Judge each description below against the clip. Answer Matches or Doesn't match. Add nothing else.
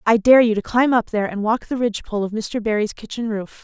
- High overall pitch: Matches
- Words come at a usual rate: Doesn't match